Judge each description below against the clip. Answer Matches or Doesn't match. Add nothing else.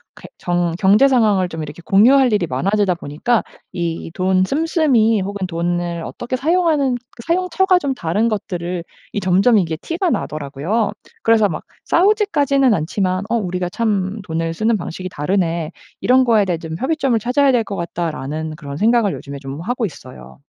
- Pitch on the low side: Doesn't match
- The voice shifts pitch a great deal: Matches